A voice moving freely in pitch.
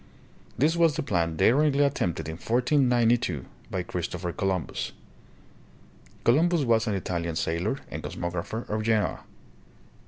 Yes: wide, 6.8 semitones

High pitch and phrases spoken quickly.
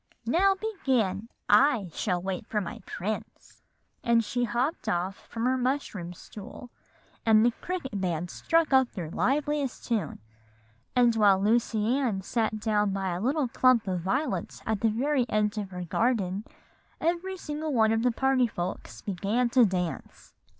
No: high, 225 Hz; average, 155 wpm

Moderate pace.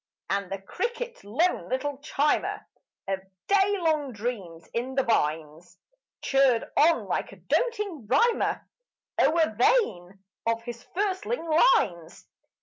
No: slow, 120 wpm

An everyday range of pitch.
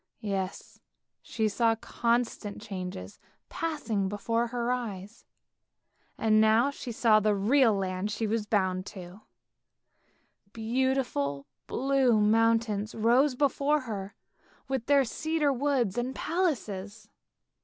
Yes: average, 3.9 semitones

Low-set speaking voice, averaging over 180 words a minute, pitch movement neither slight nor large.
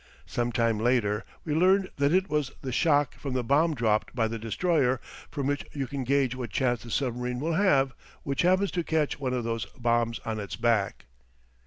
Yes: low, 130 Hz; average, 200 wpm; average, 4.1 semitones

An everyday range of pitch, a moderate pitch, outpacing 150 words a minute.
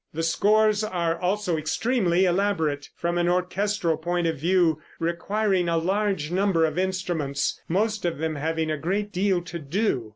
Yes: average, 3.5 semitones; medium, 175 Hz; average, 160 wpm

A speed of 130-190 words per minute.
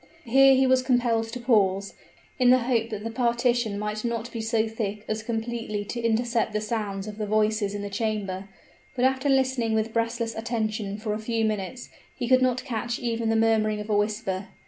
No: average, 200 wpm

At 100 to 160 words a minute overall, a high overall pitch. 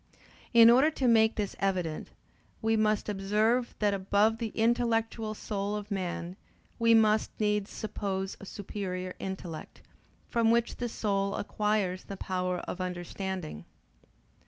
Yes: slow, 135 wpm; high, 210 Hz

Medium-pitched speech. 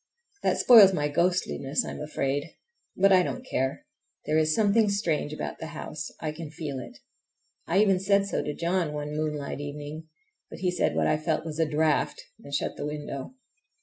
Yes: medium, 155 Hz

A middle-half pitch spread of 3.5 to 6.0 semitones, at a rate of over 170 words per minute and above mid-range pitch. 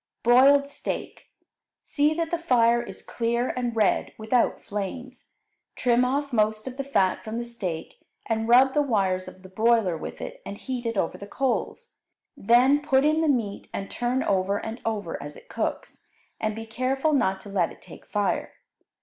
Yes: average, 4.4 semitones; average, 185 wpm; high, 235 Hz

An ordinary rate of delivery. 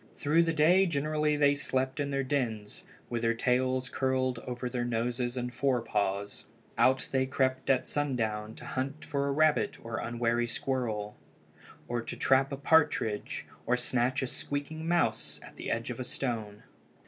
Yes: average, 165 wpm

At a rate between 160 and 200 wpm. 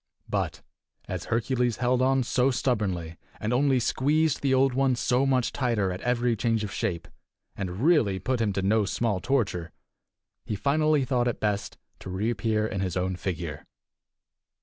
Yes: average, 170 wpm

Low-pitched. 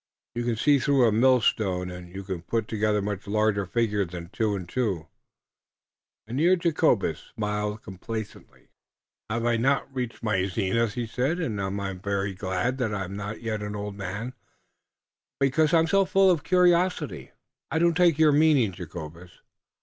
Yes: low, 110 Hz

